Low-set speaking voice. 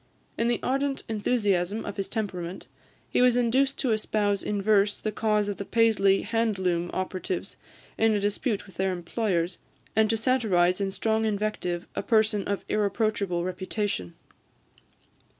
No: high, 205 Hz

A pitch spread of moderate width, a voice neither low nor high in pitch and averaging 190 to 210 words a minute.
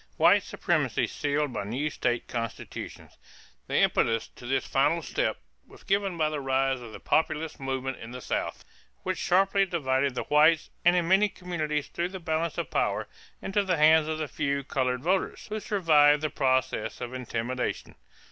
No: average, 4.6 semitones; medium, 150 Hz; average, 175 wpm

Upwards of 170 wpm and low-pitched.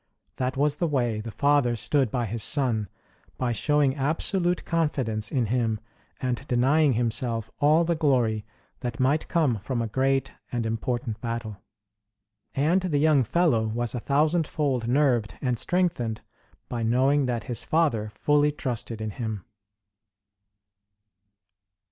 No: slow, 135 wpm; low, 125 Hz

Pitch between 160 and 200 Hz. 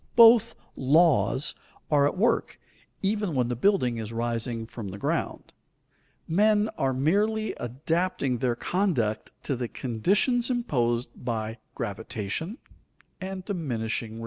No: low, 135 Hz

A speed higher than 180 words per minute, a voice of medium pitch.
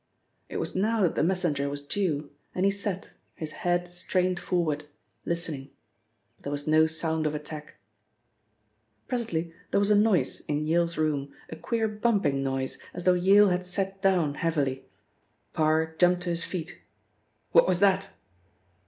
No: average, 160 wpm; medium, 170 Hz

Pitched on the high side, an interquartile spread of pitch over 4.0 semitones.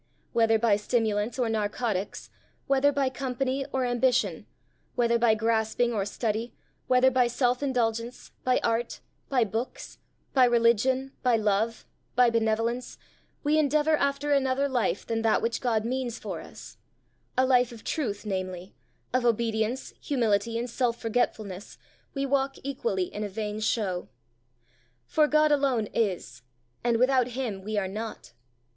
No: high, 235 Hz; average, 3.0 semitones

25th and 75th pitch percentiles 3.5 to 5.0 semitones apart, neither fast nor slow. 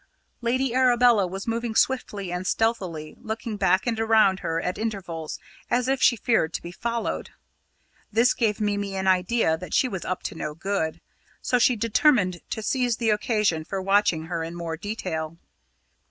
Yes: average, 4.6 semitones; average, 170 wpm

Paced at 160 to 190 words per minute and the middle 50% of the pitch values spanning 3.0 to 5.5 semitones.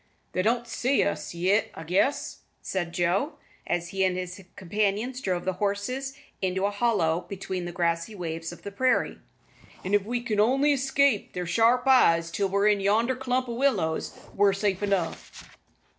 Yes: average, 175 wpm; average, 5.0 semitones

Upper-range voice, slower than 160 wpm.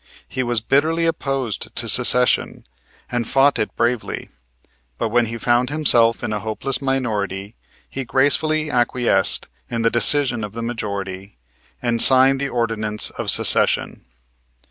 No: low, 120 Hz; average, 140 wpm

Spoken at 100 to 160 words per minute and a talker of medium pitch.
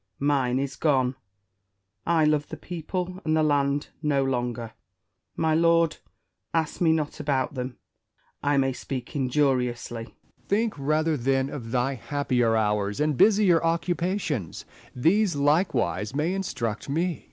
Yes: average, 140 wpm; medium, 145 Hz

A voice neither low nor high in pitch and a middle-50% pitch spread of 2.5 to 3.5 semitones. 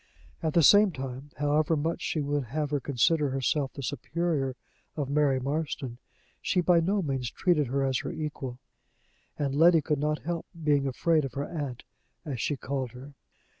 Yes: medium, 145 Hz; average, 2.8 semitones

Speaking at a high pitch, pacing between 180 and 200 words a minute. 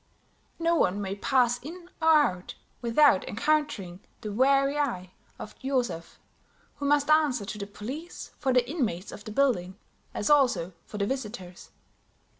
No: high, 245 Hz; average, 150 wpm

